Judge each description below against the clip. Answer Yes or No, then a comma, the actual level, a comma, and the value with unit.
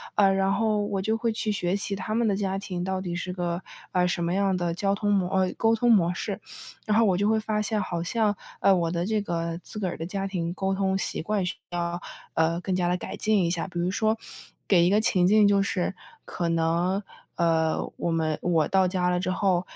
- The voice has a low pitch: No, high, 190 Hz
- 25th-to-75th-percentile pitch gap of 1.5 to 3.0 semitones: Yes, average, 2.7 semitones